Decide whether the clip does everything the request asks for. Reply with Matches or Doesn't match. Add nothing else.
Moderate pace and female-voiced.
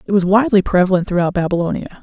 Matches